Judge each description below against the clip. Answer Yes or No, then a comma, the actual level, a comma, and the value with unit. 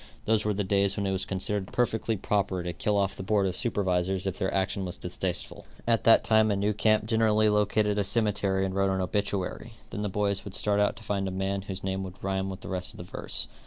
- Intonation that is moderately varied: No, narrow, 1.6 semitones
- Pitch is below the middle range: Yes, low, 100 Hz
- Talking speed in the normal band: No, fast, 245 wpm